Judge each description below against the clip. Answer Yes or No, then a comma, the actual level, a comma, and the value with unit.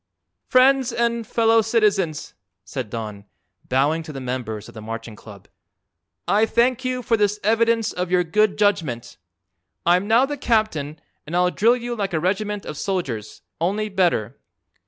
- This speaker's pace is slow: No, average, 155 wpm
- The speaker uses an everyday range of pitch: No, wide, 7.6 semitones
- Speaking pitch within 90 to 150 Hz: No, high, 195 Hz